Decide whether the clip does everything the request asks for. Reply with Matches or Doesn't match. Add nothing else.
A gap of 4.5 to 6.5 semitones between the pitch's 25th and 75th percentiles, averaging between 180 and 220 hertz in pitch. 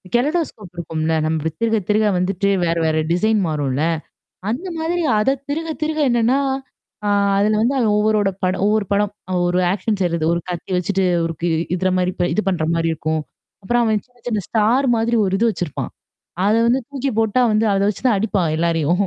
Matches